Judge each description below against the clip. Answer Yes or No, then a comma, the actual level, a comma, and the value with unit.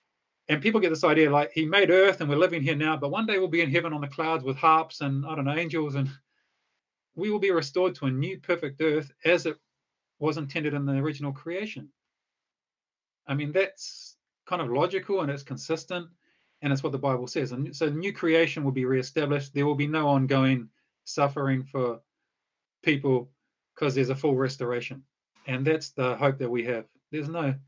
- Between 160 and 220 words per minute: Yes, fast, 205 wpm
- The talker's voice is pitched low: No, medium, 150 Hz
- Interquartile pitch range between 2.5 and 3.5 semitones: Yes, average, 3.1 semitones